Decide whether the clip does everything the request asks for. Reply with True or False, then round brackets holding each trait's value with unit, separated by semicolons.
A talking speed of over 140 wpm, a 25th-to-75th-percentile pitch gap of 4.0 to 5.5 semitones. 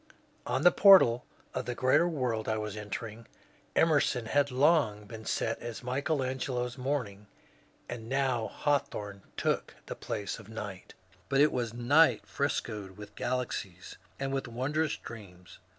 True (150 wpm; 4.3 semitones)